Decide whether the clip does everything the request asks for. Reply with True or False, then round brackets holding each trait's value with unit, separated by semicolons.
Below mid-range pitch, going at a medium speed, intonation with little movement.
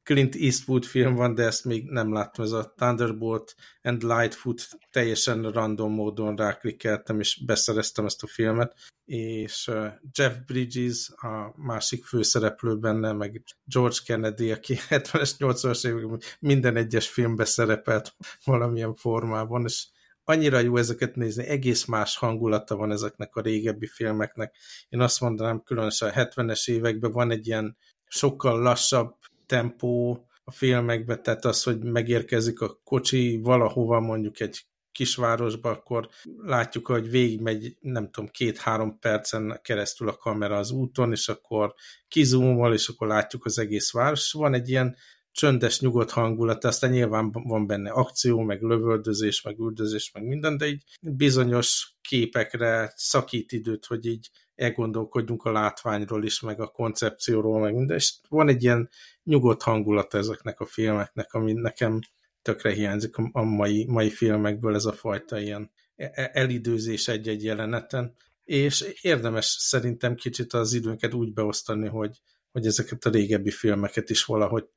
True (115 Hz; 140 wpm; 2.0 semitones)